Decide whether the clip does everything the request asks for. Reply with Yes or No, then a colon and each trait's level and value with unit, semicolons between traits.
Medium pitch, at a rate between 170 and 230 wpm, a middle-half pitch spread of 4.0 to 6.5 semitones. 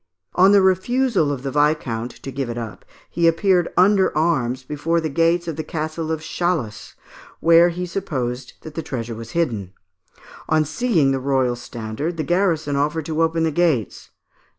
Yes: medium, 155 Hz; average, 175 wpm; average, 4.6 semitones